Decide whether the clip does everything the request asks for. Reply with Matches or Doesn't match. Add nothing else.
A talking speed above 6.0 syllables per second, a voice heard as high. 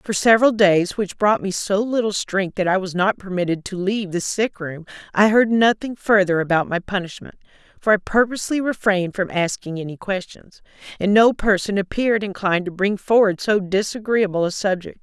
Doesn't match